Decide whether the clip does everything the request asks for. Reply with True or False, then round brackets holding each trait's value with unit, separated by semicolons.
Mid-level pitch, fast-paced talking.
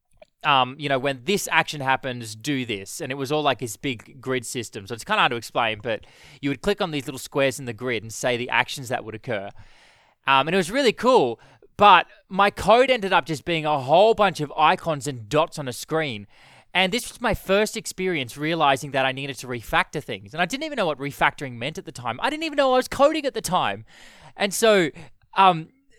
True (150 Hz; 240 wpm)